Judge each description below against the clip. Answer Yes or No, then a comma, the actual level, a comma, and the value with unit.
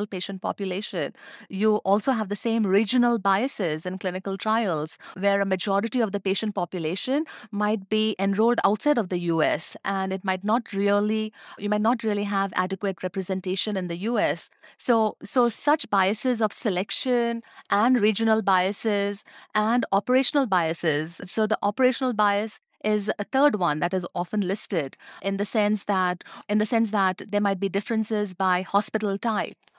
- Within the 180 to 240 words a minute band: No, average, 160 wpm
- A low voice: No, high, 205 Hz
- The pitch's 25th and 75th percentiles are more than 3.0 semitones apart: No, narrow, 2.4 semitones